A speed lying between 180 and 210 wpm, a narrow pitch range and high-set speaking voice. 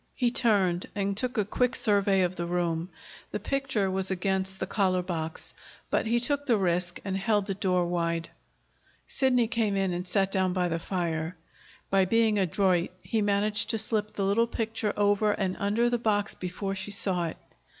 No: average, 185 wpm; average, 3.0 semitones; high, 195 Hz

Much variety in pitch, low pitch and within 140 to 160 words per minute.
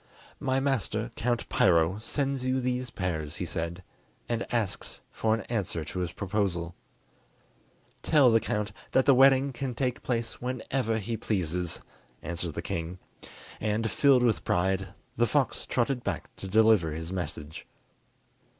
Yes: wide, 5.7 semitones; low, 110 Hz; average, 145 wpm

